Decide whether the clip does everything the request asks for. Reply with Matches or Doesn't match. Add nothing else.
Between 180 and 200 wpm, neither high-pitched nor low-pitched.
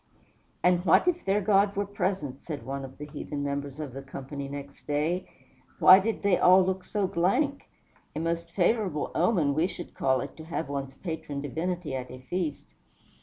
Matches